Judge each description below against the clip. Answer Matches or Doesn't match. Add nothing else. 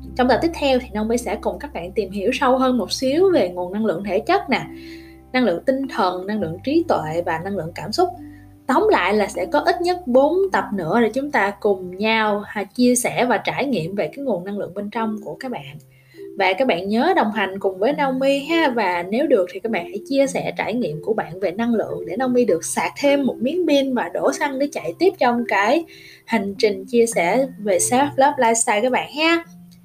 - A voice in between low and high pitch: Doesn't match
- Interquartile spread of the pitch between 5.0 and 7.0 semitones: Matches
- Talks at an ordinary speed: Matches